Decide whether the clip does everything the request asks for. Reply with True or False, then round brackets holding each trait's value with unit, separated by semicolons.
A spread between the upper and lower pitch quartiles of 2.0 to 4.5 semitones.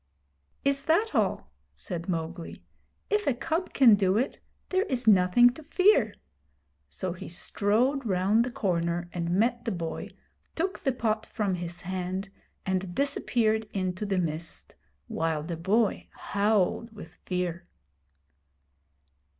False (5.3 semitones)